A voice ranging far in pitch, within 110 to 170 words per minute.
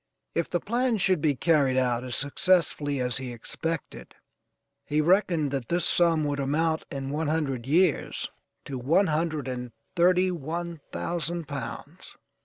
No: average, 4.0 semitones; average, 150 wpm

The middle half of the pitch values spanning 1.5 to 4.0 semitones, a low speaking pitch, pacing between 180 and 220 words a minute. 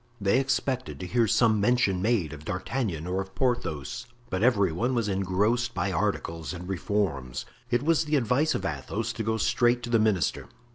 No: average, 5.0 semitones; low, 105 Hz; average, 185 wpm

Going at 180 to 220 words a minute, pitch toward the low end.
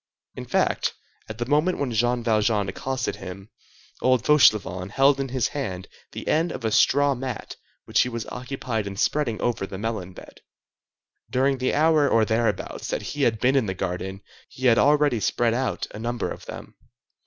Yes: average, 185 wpm; low, 120 Hz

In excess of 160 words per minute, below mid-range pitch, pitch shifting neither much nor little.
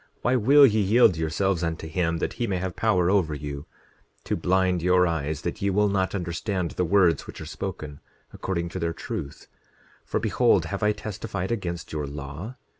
Yes: average, 190 wpm; very low, 90 Hz; average, 3.6 semitones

